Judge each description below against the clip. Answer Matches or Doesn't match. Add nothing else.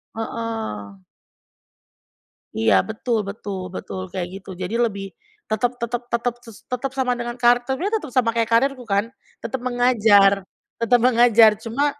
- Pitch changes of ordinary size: Matches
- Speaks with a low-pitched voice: Doesn't match